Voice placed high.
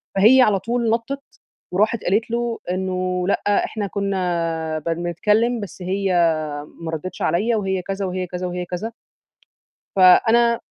Yes: high, 195 Hz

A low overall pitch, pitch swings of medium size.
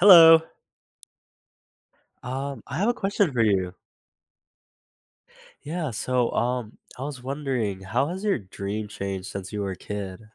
No: low, 125 Hz; wide, 6.7 semitones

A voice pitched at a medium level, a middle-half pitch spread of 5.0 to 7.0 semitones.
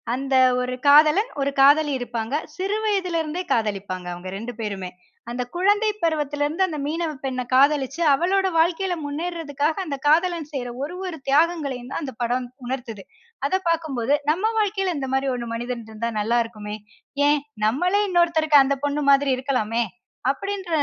No: very high, 290 Hz; average, 5.3 semitones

